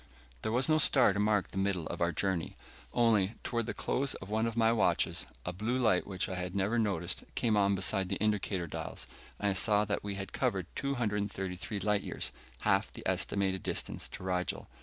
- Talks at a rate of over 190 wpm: Yes, average, 200 wpm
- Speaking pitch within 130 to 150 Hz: No, low, 100 Hz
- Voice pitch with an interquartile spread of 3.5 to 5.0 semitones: No, average, 2.8 semitones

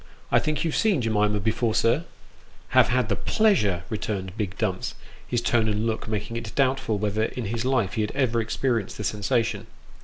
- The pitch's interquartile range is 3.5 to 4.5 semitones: No, average, 2.9 semitones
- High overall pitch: No, low, 110 Hz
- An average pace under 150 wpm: No, average, 195 wpm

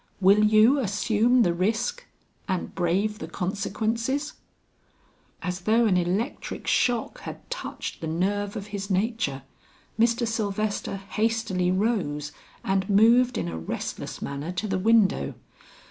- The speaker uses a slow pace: Yes, slow, 130 wpm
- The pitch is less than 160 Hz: No, high, 205 Hz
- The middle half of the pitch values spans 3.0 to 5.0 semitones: Yes, average, 3.7 semitones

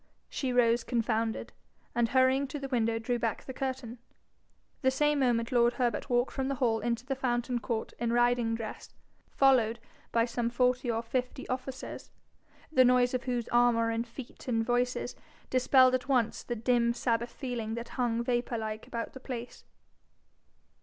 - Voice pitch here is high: Yes, high, 245 Hz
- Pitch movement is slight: Yes, narrow, 1.7 semitones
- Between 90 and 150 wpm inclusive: No, average, 165 wpm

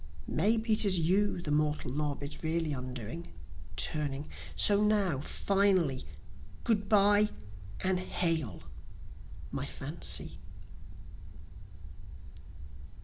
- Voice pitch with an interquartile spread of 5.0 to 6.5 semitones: Yes, wide, 5.5 semitones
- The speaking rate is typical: No, slow, 90 wpm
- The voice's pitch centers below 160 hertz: No, medium, 170 Hz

